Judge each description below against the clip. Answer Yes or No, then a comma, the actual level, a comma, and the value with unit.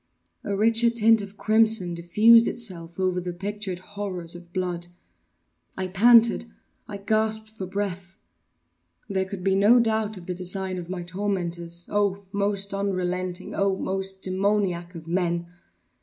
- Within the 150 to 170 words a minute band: No, average, 140 wpm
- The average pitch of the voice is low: No, high, 190 Hz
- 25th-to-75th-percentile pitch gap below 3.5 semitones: Yes, narrow, 2.5 semitones